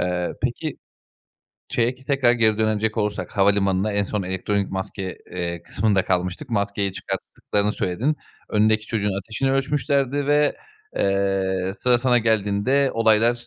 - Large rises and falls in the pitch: No, average, 3.7 semitones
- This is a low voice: Yes, low, 105 Hz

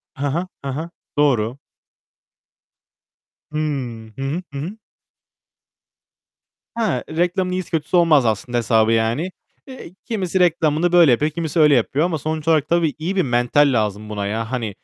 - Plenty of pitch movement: Yes, wide, 6.1 semitones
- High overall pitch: No, medium, 150 Hz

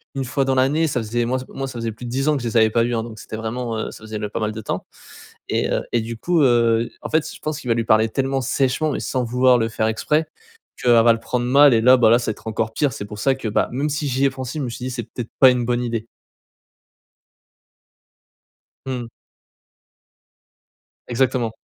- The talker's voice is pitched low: Yes, low, 120 Hz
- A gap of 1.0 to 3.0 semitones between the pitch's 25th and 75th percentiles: Yes, average, 2.7 semitones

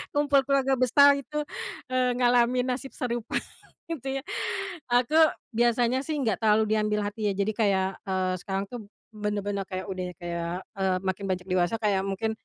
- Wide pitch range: No, average, 4.5 semitones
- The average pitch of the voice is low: No, high, 215 Hz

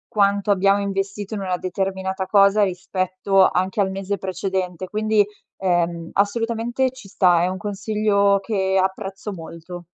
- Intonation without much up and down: Yes, narrow, 1.5 semitones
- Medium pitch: No, high, 195 Hz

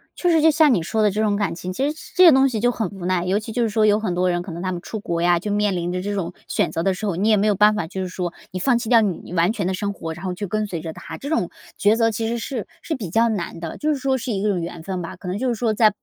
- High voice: Yes, high, 205 Hz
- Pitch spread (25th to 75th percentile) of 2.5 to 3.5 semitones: No, average, 4.0 semitones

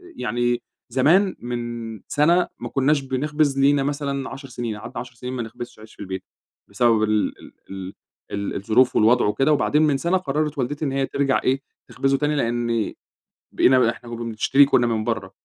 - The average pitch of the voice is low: Yes, low, 125 Hz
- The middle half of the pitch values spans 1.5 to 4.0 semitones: Yes, average, 3.5 semitones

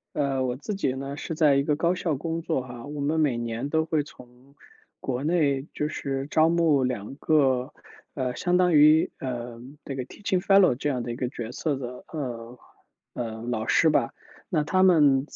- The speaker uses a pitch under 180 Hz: Yes, medium, 140 Hz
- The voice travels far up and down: No, average, 4.0 semitones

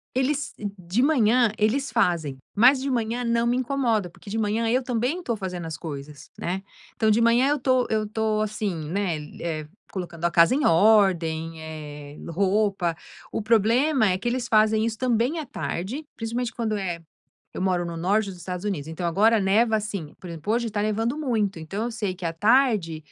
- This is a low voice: No, high, 215 Hz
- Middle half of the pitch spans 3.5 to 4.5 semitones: No, average, 5.1 semitones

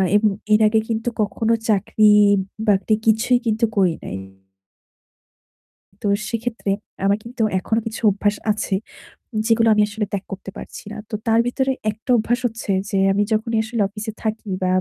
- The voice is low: No, high, 215 Hz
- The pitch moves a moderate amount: No, narrow, 1.8 semitones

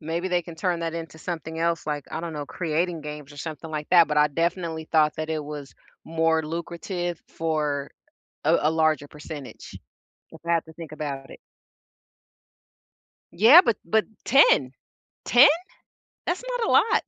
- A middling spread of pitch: No, narrow, 2.1 semitones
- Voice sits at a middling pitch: Yes, medium, 160 Hz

